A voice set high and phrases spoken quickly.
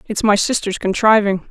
No: high, 205 Hz; average, 160 wpm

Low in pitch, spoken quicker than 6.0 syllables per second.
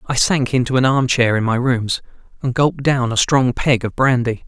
No: low, 125 Hz; 5.0 syllables/s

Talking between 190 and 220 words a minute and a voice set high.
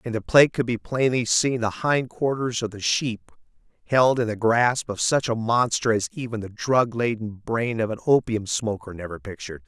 No: fast, 205 wpm; low, 115 Hz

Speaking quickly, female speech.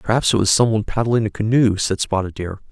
No: fast, 245 wpm; male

